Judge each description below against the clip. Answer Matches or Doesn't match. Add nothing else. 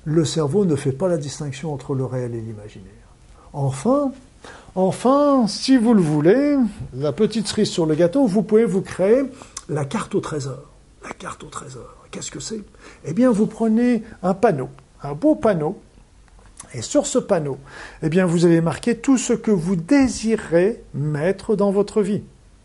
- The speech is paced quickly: Doesn't match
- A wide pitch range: Matches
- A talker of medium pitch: Doesn't match